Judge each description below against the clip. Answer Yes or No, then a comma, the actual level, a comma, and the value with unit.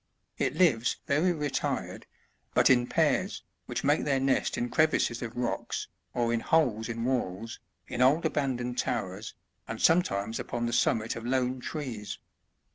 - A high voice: No, low, 125 Hz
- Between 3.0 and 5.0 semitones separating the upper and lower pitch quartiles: Yes, average, 3.5 semitones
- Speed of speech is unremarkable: Yes, average, 155 wpm